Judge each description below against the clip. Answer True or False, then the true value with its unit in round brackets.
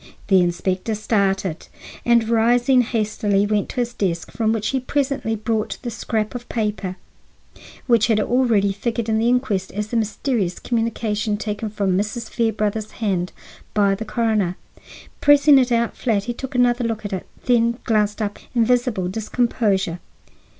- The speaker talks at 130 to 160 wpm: True (155 wpm)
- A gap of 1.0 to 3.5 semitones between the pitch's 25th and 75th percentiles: True (2.7 semitones)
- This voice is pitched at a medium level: False (220 Hz)